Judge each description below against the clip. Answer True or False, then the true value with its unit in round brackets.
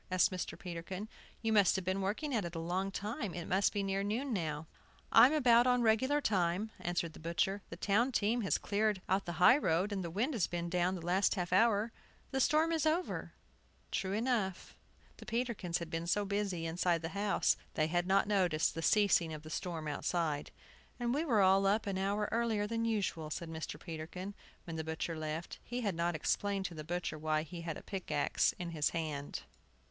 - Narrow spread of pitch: False (4.2 semitones)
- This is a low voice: False (190 Hz)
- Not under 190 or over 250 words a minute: True (205 wpm)